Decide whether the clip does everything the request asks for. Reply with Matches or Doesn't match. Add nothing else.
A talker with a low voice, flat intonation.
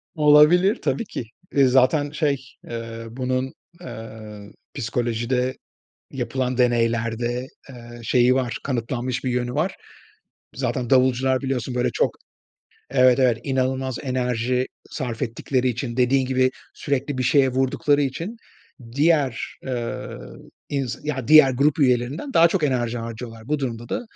Matches